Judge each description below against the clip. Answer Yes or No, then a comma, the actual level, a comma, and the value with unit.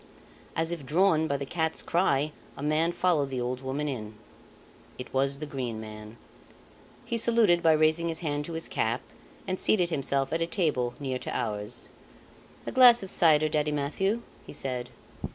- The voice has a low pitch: No, medium, 150 Hz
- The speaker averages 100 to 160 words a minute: No, average, 175 wpm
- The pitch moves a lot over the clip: No, average, 4.2 semitones